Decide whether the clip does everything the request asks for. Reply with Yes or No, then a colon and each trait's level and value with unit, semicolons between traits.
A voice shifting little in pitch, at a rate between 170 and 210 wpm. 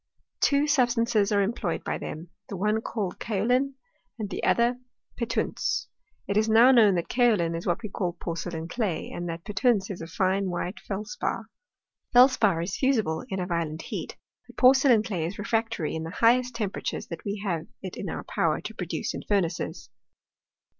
No: average, 5.1 semitones; average, 175 wpm